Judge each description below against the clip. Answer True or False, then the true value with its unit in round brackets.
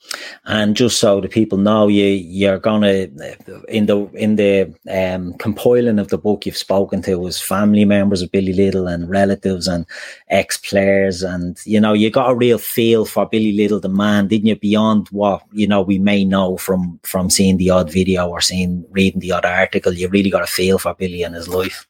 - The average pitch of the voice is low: True (100 Hz)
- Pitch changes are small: True (2.0 semitones)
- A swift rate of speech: True (210 wpm)